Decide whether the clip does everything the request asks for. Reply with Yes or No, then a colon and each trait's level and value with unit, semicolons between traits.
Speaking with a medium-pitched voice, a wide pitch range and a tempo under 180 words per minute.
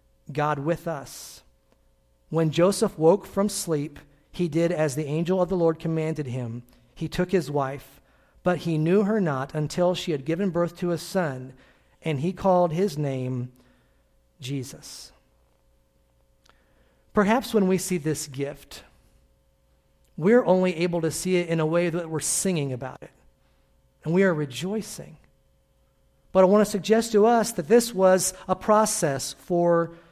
Yes: medium, 165 Hz; wide, 6.3 semitones; average, 155 wpm